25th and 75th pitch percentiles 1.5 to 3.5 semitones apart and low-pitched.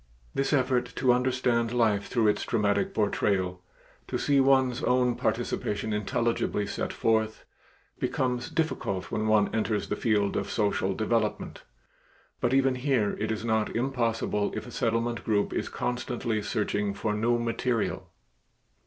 Yes: average, 2.9 semitones; low, 115 Hz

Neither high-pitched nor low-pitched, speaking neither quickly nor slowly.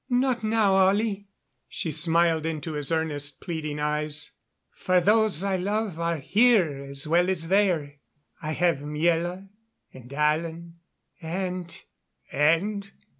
No: medium, 170 Hz; slow, 125 wpm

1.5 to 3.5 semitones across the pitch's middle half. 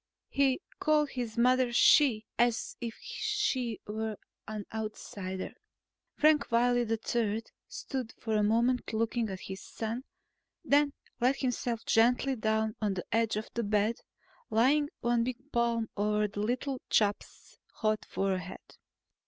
Yes: narrow, 2.6 semitones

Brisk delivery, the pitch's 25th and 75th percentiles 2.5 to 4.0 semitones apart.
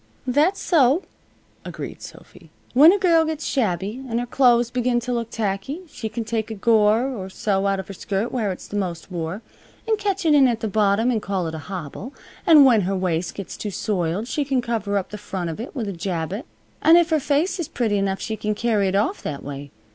No: fast, 230 wpm; average, 5.2 semitones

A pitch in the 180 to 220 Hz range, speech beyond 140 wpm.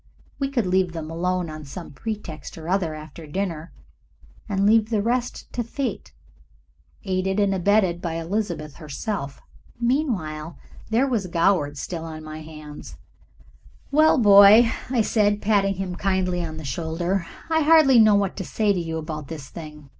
Yes: medium, 185 Hz; average, 160 wpm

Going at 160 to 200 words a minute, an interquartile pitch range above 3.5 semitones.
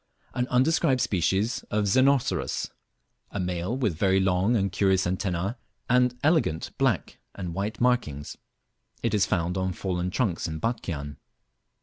No: slow, 135 wpm; wide, 5.6 semitones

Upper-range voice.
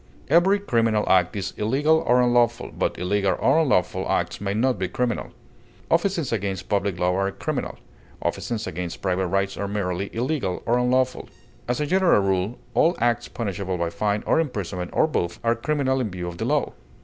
No: low, 110 Hz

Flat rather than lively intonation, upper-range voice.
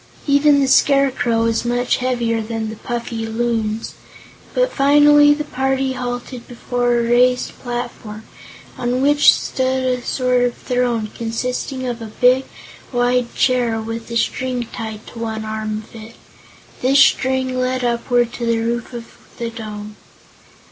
Yes: narrow, 2.1 semitones; high, 245 Hz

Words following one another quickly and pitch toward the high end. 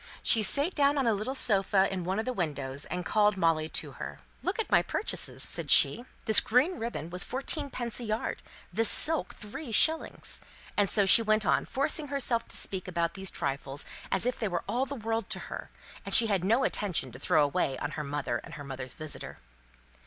Yes: fast, 210 wpm; high, 210 Hz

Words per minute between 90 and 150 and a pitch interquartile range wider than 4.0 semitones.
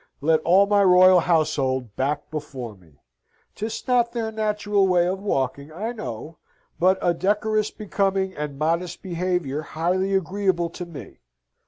Yes: average, 145 wpm; average, 4.7 semitones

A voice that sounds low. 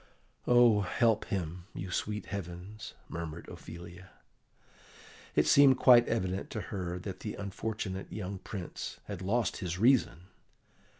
Yes: very low, 95 Hz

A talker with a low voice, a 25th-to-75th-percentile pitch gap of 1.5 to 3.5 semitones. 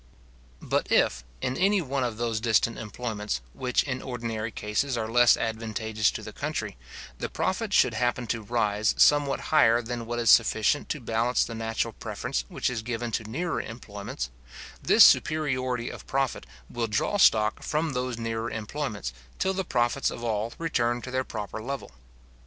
Yes: low, 120 Hz; narrow, 2.6 semitones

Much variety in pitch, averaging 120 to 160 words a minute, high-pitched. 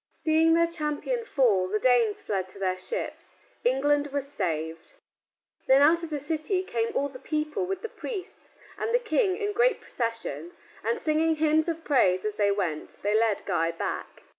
No: wide, 8.0 semitones; average, 175 wpm; very high, 290 Hz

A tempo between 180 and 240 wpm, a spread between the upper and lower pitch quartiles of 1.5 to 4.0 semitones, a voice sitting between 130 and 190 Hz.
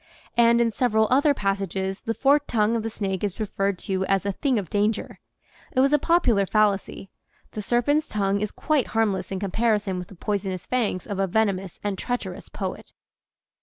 No: average, 185 wpm; average, 3.3 semitones; high, 210 Hz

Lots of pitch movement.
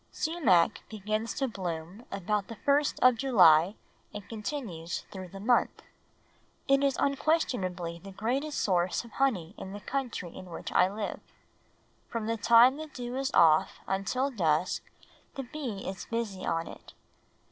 Yes: wide, 6.1 semitones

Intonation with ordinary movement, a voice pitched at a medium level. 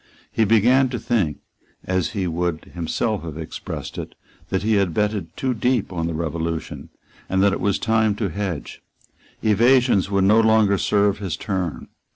No: average, 4.2 semitones; low, 100 Hz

